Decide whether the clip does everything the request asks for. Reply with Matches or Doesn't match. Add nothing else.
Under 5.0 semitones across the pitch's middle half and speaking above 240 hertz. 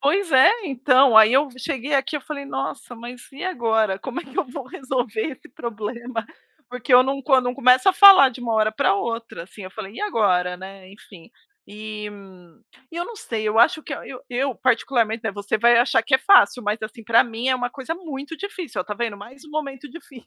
Matches